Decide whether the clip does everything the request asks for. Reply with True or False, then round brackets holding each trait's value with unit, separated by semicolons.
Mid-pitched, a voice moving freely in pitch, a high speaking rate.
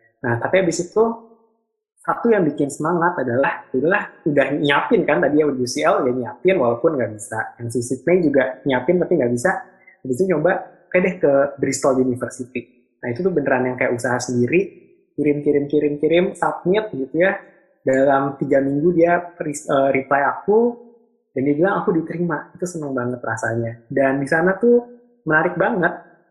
True (155 Hz; 5.8 semitones; 175 wpm)